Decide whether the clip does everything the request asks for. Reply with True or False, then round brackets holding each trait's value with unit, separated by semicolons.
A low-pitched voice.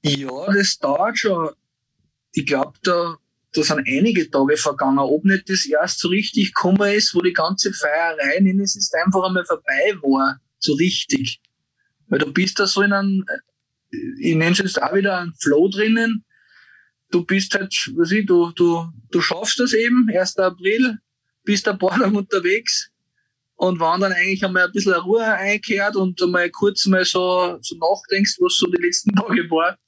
False (195 Hz)